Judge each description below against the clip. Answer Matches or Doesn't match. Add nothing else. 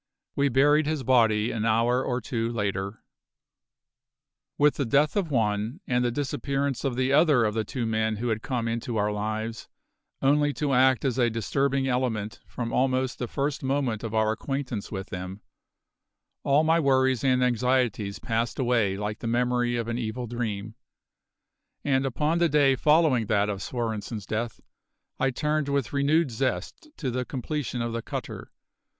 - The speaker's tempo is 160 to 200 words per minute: Matches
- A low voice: Matches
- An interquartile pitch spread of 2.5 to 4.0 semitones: Matches